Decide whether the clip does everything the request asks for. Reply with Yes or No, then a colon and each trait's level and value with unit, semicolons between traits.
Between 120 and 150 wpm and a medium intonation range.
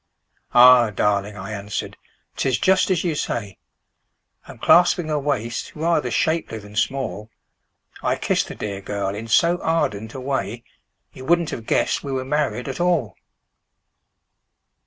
No: average, 145 wpm; wide, 6.6 semitones